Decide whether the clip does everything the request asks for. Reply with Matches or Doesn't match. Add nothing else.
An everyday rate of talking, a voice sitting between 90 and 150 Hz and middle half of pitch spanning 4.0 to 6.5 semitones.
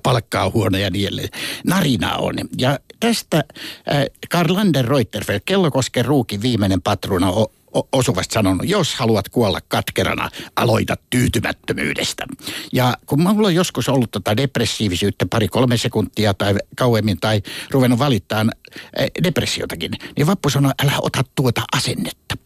Matches